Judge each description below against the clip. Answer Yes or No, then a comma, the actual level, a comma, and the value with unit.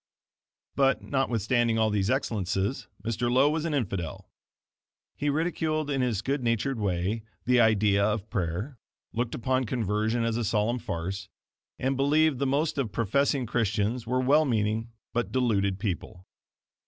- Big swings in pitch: No, average, 4.3 semitones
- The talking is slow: No, average, 150 wpm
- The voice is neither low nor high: No, low, 115 Hz